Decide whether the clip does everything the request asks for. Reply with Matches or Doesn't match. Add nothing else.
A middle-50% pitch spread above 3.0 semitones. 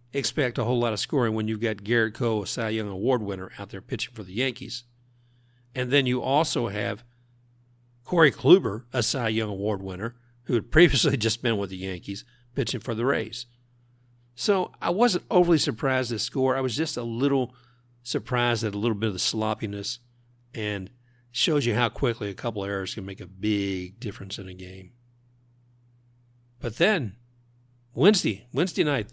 Doesn't match